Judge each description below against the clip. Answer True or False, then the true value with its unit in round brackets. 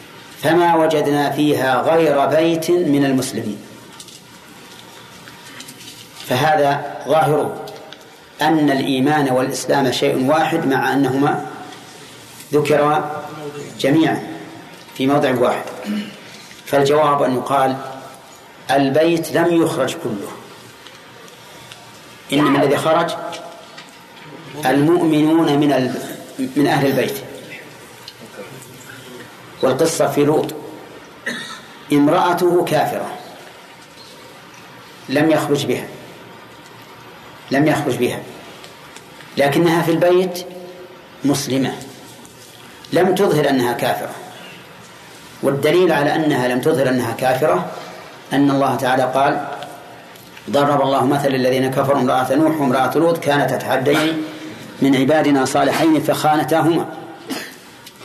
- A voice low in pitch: False (145 Hz)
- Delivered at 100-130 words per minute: False (85 wpm)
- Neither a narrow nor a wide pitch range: True (3.0 semitones)